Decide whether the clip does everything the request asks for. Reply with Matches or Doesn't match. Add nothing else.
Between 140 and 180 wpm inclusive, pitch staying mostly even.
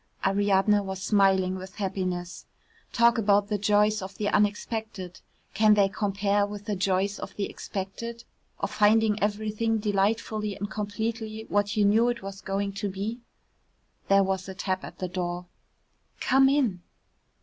Matches